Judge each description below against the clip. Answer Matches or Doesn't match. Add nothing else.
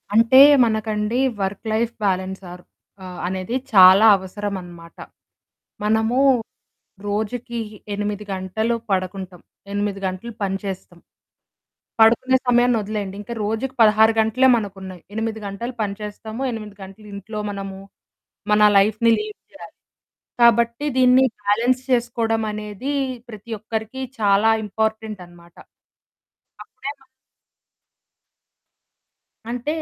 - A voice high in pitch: Matches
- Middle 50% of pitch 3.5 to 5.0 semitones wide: Doesn't match